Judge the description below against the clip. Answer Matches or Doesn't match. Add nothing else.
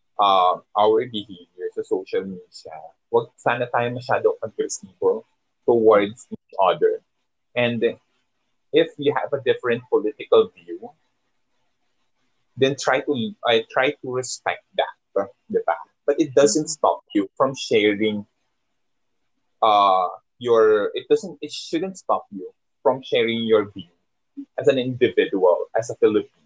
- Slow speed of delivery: Doesn't match